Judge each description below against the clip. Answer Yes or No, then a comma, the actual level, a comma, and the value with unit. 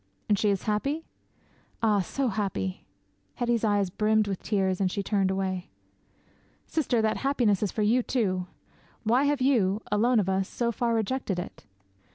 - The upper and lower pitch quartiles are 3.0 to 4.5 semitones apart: Yes, average, 3.7 semitones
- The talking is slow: No, average, 165 wpm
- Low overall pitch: No, high, 210 Hz